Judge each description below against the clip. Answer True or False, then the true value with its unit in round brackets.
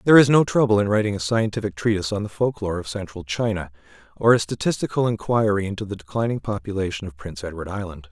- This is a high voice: False (105 Hz)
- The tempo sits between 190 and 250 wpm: True (205 wpm)